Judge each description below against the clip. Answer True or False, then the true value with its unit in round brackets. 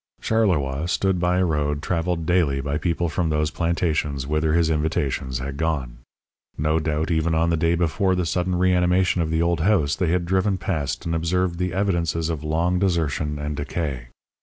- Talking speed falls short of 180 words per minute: False (185 wpm)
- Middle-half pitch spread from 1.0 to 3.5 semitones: True (2.8 semitones)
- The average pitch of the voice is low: True (80 Hz)